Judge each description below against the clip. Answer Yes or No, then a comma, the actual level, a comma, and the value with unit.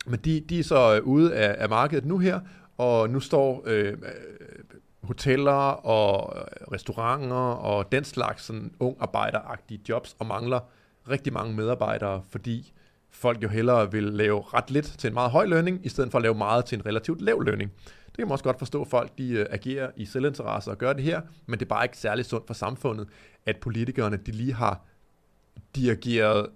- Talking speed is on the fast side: No, average, 190 wpm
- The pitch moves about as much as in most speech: Yes, average, 4.0 semitones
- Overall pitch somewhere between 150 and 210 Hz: No, low, 120 Hz